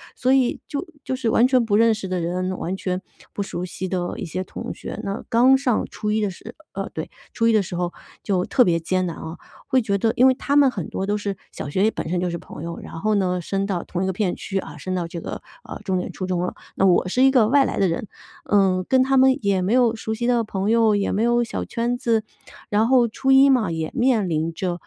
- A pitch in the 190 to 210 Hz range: Yes, high, 205 Hz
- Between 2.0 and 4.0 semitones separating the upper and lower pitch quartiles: No, average, 4.7 semitones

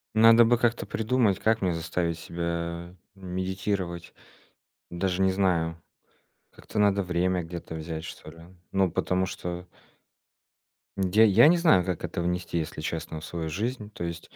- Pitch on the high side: No, very low, 90 Hz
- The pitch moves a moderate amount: Yes, average, 3.0 semitones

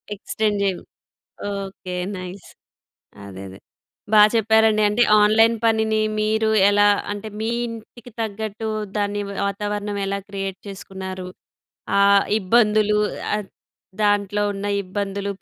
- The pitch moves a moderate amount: No, narrow, 1.8 semitones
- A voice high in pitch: Yes, high, 205 Hz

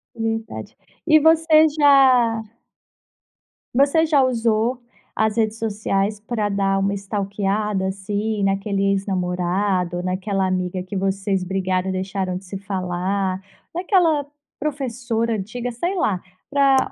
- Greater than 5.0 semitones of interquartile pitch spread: No, average, 4.1 semitones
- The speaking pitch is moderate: No, high, 205 Hz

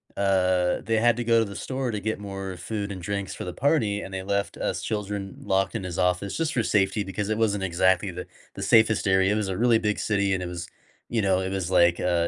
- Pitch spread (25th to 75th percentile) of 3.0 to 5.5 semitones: No, narrow, 2.5 semitones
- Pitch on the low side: Yes, low, 100 Hz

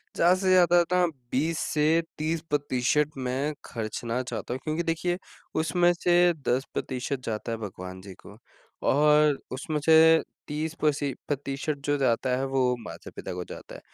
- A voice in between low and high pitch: Yes, medium, 145 Hz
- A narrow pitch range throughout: No, average, 4.3 semitones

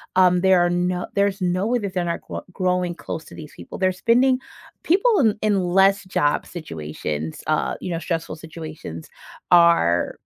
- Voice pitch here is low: No, medium, 180 Hz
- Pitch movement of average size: Yes, average, 3.2 semitones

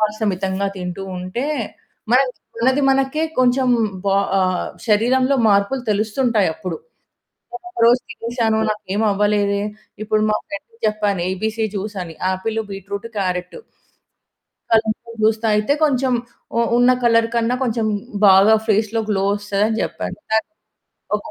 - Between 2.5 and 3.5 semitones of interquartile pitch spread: Yes, average, 2.9 semitones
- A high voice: Yes, high, 215 Hz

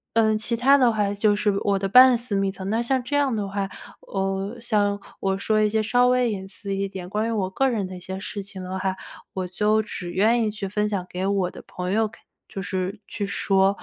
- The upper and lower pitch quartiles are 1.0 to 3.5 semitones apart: Yes, narrow, 2.5 semitones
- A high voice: Yes, high, 205 Hz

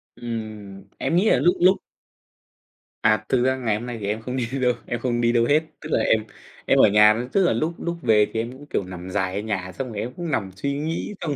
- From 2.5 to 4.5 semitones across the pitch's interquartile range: No, average, 4.9 semitones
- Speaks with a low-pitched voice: Yes, low, 120 Hz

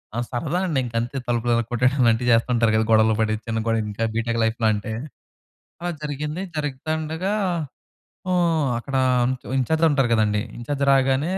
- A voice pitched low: Yes, low, 125 Hz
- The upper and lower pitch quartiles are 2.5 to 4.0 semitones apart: No, average, 4.8 semitones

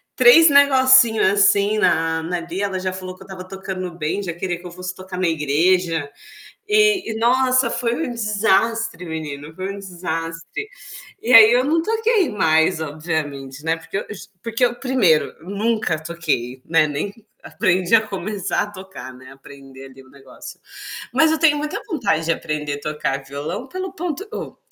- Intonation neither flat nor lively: No, wide, 6.4 semitones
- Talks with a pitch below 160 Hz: No, medium, 185 Hz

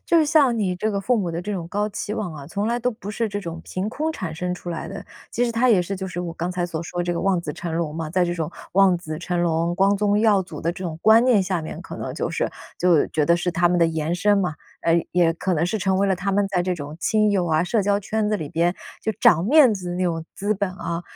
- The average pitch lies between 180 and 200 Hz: Yes, medium, 185 Hz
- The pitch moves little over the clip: No, average, 3.4 semitones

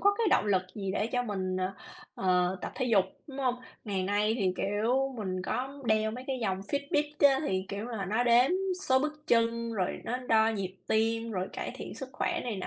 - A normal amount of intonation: Yes, average, 4.7 semitones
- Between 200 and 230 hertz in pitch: Yes, high, 220 Hz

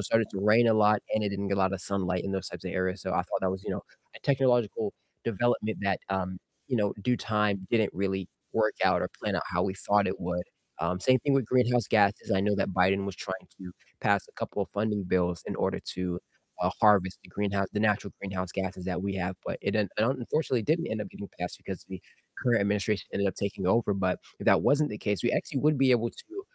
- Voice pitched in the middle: No, low, 100 Hz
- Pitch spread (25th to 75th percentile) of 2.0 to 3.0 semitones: Yes, average, 2.7 semitones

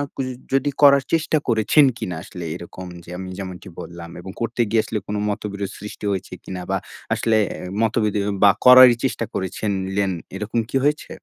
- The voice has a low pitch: Yes, low, 105 Hz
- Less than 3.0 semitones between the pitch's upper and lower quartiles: No, average, 4.4 semitones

